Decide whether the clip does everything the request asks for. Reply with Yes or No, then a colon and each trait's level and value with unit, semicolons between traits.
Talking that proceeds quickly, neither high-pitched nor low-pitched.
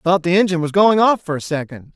Yes: fast, 275 wpm; medium, 175 Hz